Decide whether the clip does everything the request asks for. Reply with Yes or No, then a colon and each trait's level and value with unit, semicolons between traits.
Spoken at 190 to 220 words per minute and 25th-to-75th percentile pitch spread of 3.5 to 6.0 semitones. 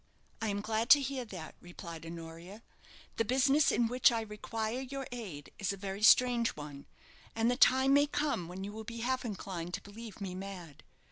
Yes: average, 195 wpm; average, 5.1 semitones